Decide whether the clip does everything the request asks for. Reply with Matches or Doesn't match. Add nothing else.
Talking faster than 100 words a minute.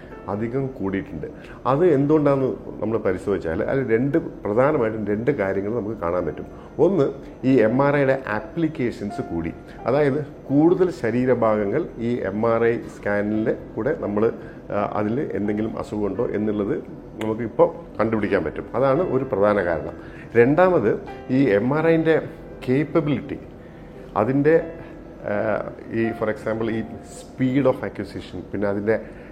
Matches